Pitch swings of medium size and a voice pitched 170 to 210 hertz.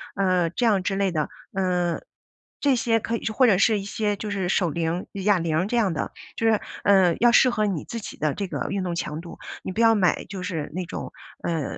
Yes: average, 3.5 semitones; high, 195 Hz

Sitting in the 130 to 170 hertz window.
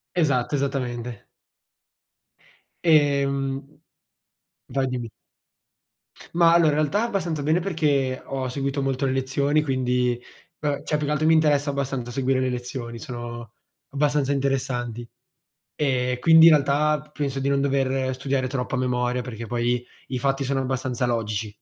Yes: low, 135 Hz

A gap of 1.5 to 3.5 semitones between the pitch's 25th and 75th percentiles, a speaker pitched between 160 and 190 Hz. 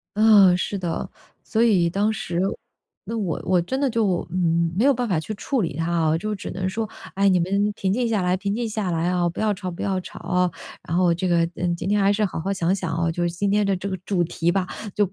Yes: average, 3.1 semitones; medium, 185 Hz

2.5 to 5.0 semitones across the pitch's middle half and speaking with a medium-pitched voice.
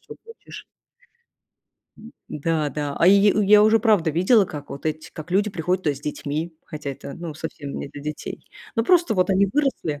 No: wide, 5.6 semitones; medium, 170 Hz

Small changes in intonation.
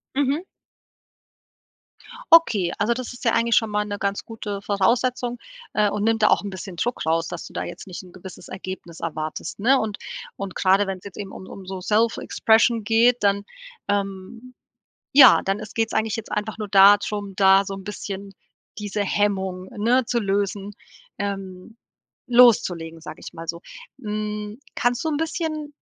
No: average, 3.1 semitones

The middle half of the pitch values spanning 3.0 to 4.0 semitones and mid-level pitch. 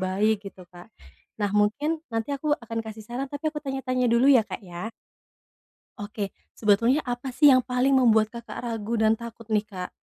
No: average, 3.7 semitones; high, 230 Hz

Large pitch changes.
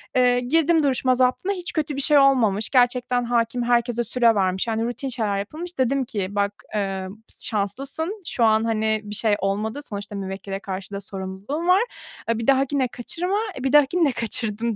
No: average, 4.9 semitones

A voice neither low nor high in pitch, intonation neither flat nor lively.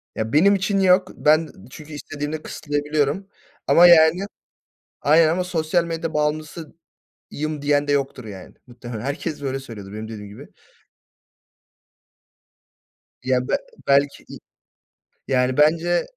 Yes: medium, 150 Hz; average, 3.9 semitones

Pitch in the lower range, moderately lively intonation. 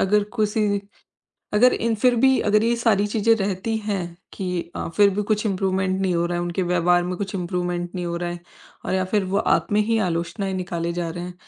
No: high, 190 Hz; average, 3.0 semitones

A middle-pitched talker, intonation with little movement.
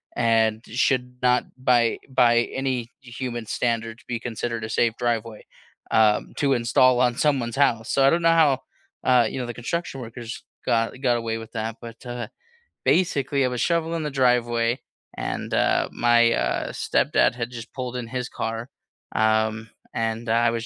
No: low, 120 Hz; narrow, 2.0 semitones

